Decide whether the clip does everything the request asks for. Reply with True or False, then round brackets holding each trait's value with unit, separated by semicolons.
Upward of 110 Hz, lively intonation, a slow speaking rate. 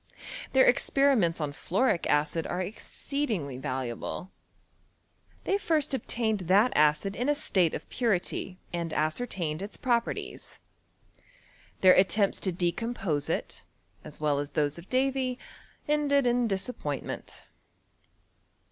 True (190 Hz; 8.0 semitones; 120 wpm)